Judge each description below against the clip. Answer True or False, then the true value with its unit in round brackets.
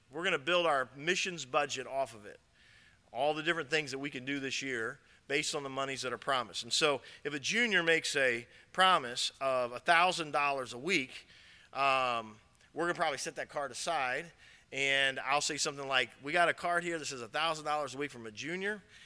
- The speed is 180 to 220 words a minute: True (200 wpm)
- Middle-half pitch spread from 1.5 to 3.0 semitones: False (3.8 semitones)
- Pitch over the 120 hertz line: True (140 Hz)